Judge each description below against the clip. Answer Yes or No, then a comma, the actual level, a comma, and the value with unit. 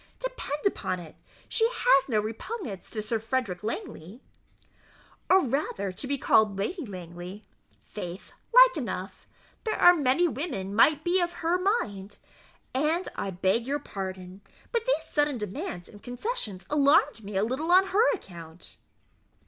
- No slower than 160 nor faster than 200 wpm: No, average, 150 wpm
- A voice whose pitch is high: Yes, very high, 255 Hz